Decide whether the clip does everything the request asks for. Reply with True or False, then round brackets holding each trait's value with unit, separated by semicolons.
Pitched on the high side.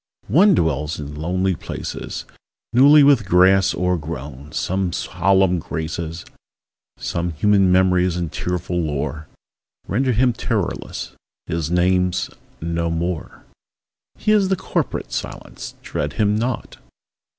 False (90 Hz)